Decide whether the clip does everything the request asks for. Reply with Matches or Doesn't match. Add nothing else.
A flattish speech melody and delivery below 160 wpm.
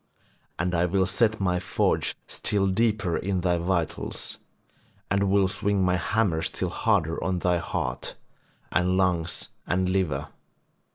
Matches